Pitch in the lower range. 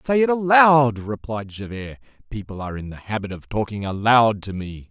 Yes: low, 115 Hz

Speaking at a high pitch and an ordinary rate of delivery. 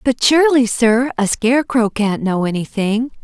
Yes: high, 235 Hz; average, 150 wpm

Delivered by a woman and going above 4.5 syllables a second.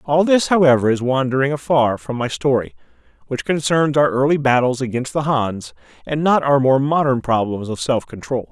No: male; 5.2 syllables/s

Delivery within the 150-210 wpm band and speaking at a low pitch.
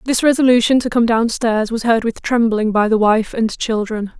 No: average, 200 wpm; high, 230 Hz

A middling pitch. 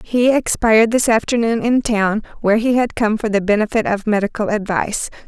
No: high, 220 Hz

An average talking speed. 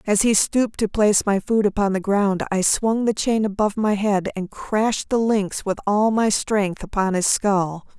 No: fast, 210 wpm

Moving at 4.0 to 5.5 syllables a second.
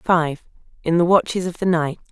No: 6.5 syllables/s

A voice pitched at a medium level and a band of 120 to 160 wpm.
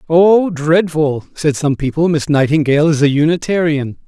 Yes: medium, 155 Hz; average, 145 wpm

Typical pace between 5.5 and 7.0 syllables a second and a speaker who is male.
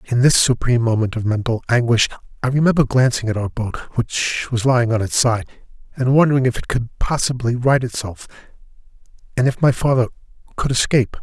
Yes: 5.7 syllables/s; male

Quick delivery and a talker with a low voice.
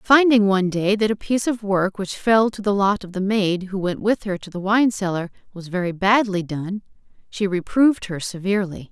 No: fast, 215 wpm; high, 200 Hz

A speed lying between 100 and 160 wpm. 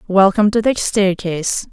Yes: average, 140 wpm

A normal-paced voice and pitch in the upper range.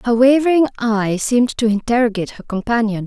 Yes: average, 155 wpm; high, 230 Hz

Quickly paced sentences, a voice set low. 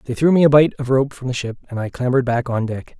Yes: fast, 320 wpm; low, 130 Hz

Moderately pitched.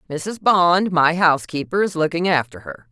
Yes: medium, 165 Hz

